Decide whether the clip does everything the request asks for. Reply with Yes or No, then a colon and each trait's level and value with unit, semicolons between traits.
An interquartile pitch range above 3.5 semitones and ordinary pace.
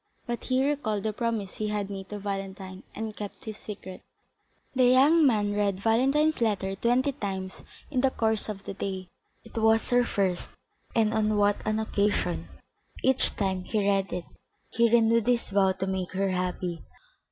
No: average, 3.2 semitones; average, 175 wpm